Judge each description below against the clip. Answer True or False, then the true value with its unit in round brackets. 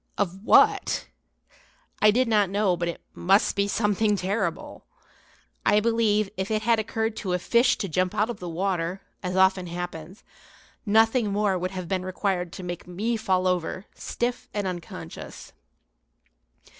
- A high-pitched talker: True (195 Hz)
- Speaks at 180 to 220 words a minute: False (155 wpm)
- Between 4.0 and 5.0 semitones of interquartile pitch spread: False (2.9 semitones)